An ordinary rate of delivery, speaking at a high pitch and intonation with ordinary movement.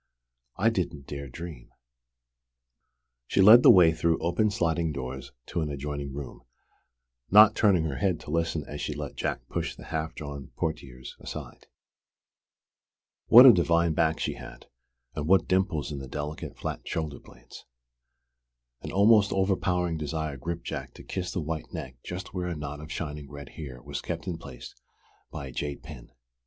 No: average, 170 wpm; very low, 80 Hz; average, 3.8 semitones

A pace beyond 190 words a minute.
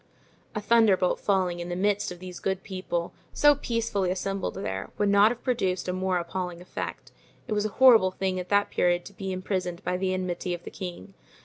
Yes: fast, 205 wpm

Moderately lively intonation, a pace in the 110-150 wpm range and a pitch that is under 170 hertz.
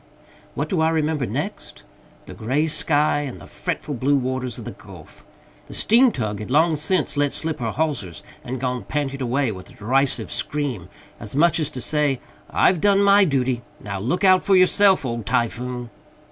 No: average, 4.4 semitones; average, 185 wpm; medium, 140 Hz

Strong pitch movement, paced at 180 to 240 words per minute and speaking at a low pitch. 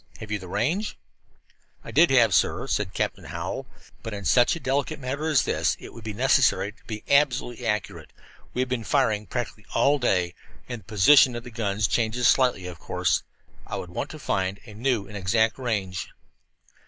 No: average, 4.1 semitones; average, 190 wpm; low, 115 Hz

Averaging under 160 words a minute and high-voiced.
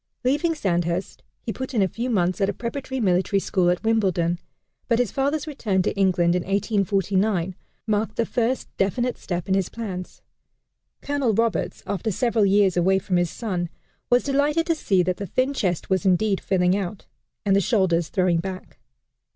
No: average, 175 wpm; high, 195 Hz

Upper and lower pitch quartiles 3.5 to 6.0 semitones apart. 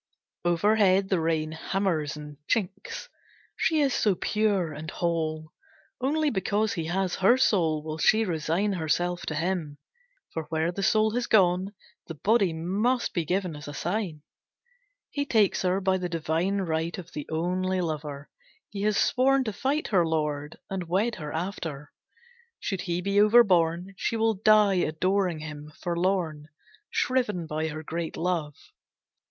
Yes: average, 4.2 semitones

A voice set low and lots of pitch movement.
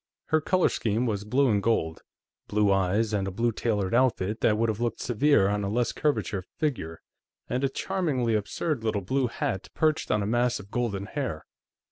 No: low, 115 Hz; average, 4.1 semitones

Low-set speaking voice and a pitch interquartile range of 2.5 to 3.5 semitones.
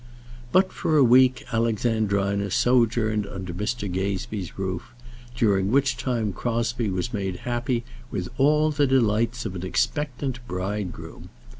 No: low, 115 Hz; average, 3.9 semitones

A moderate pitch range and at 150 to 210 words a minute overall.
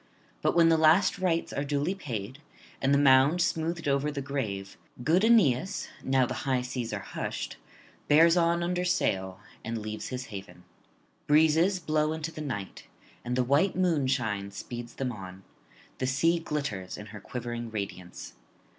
No: wide, 6.0 semitones; average, 160 wpm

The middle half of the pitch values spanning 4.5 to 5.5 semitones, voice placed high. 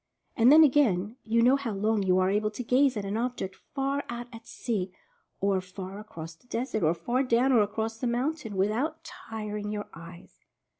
No: average, 4.0 semitones; high, 220 Hz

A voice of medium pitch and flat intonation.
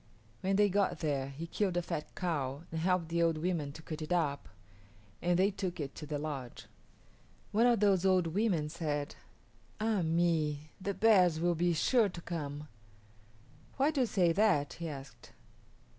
No: medium, 170 Hz; average, 3.9 semitones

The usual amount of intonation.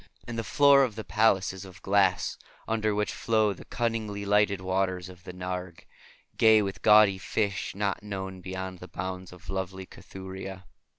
No: narrow, 2.2 semitones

